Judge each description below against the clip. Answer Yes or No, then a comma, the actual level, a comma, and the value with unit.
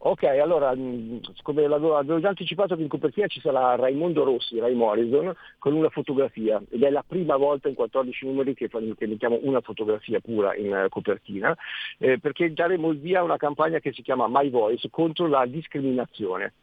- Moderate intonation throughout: Yes, average, 4.5 semitones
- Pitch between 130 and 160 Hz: Yes, medium, 140 Hz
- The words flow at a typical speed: No, fast, 175 wpm